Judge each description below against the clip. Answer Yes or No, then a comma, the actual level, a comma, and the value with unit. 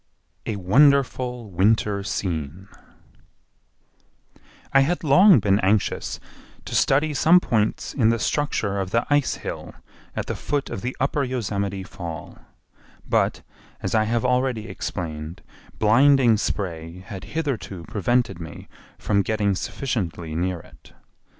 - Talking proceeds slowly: Yes, slow, 125 wpm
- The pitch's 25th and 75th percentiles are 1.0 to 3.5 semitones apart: No, wide, 5.6 semitones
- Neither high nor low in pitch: No, low, 110 Hz